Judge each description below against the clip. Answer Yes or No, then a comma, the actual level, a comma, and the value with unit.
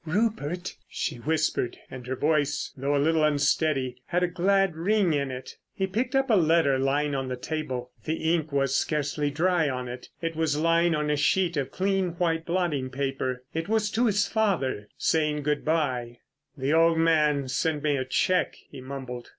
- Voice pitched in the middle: Yes, medium, 155 Hz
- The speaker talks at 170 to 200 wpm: Yes, average, 185 wpm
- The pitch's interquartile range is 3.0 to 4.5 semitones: Yes, average, 3.9 semitones